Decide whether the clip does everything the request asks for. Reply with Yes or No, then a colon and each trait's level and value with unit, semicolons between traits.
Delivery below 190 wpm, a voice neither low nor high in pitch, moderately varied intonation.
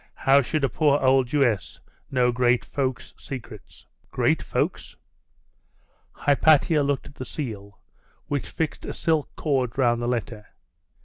No: average, 140 wpm; low, 130 Hz; average, 3.0 semitones